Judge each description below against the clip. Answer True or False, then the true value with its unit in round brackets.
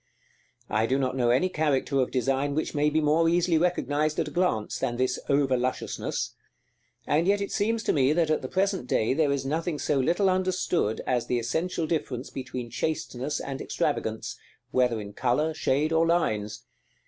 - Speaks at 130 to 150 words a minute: False (185 wpm)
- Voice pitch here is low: False (145 Hz)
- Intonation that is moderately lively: True (4.5 semitones)